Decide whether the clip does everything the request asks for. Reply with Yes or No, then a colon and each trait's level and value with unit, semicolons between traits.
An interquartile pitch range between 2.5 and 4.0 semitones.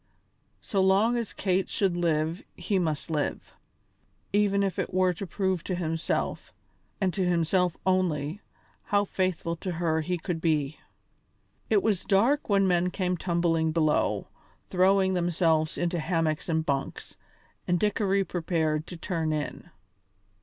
Yes: average, 2.9 semitones